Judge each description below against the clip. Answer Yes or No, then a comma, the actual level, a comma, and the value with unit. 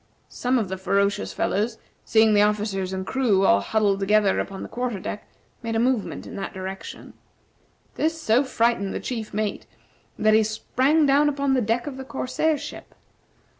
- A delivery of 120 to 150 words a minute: No, average, 175 wpm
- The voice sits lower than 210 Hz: No, high, 220 Hz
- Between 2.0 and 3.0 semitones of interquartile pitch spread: No, average, 4.4 semitones